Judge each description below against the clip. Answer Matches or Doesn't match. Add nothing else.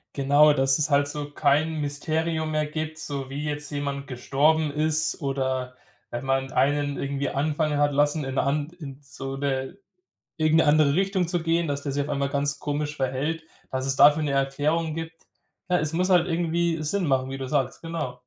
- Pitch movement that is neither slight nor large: Doesn't match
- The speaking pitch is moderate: Matches